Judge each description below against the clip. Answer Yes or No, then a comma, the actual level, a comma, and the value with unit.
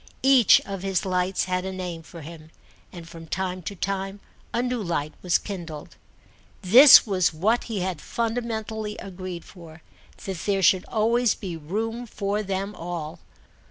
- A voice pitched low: No, high, 190 Hz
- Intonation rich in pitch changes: No, average, 3.7 semitones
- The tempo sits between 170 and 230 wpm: No, average, 160 wpm